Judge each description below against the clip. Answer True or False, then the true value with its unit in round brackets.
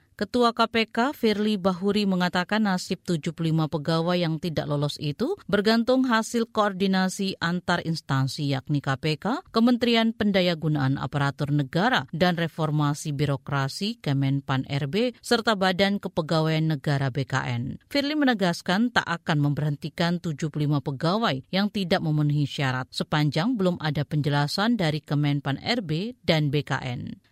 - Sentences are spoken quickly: False (115 wpm)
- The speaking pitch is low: False (170 Hz)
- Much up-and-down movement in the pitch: True (5.7 semitones)